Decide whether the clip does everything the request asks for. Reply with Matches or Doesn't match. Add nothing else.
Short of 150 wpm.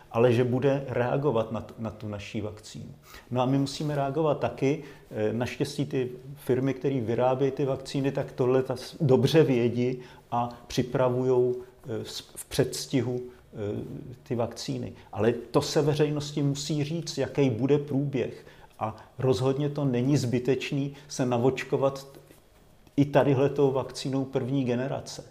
Matches